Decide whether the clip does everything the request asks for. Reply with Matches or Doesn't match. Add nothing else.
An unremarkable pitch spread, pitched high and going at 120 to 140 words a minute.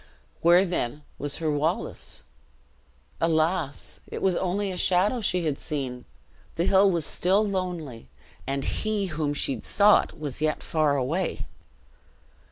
Doesn't match